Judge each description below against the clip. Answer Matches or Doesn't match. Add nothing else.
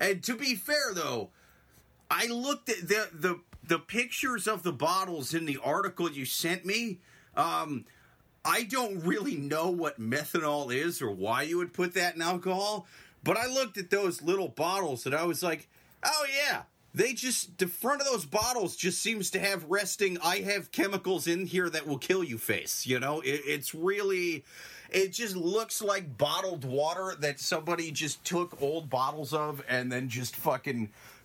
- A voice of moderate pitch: Matches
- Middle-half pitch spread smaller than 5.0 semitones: Doesn't match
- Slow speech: Doesn't match